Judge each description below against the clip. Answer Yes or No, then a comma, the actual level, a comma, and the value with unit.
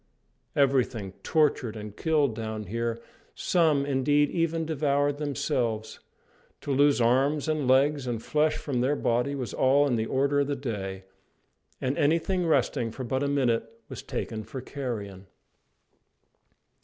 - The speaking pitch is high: No, low, 135 Hz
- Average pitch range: Yes, average, 3.9 semitones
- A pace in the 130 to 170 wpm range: Yes, average, 145 wpm